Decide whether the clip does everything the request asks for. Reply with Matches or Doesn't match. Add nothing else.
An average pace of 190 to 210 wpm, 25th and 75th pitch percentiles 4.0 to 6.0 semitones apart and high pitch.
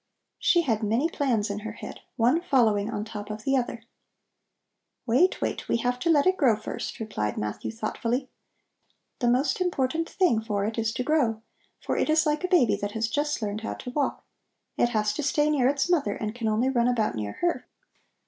Matches